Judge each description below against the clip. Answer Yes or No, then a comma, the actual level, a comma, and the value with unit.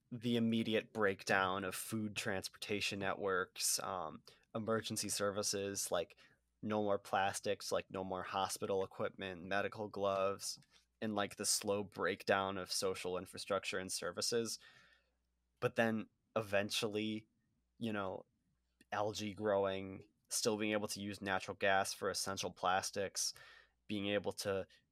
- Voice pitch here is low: Yes, low, 100 Hz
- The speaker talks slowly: Yes, slow, 125 wpm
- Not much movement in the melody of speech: Yes, narrow, 2.0 semitones